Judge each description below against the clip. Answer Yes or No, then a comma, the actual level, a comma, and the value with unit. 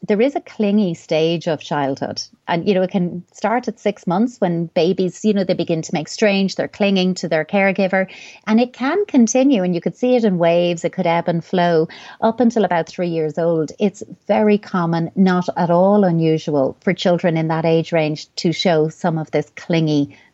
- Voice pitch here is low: No, medium, 180 Hz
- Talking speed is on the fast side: Yes, fast, 210 wpm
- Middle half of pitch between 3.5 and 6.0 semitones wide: Yes, average, 3.8 semitones